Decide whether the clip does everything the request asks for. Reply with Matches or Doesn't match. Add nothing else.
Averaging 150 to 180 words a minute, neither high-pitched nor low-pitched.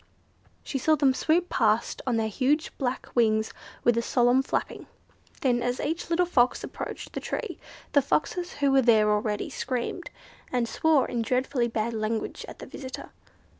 Doesn't match